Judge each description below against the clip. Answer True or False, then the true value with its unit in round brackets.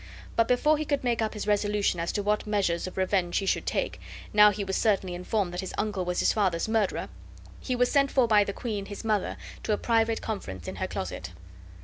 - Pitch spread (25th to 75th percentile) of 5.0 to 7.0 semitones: False (3.0 semitones)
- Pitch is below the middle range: False (210 Hz)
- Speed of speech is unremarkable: False (230 wpm)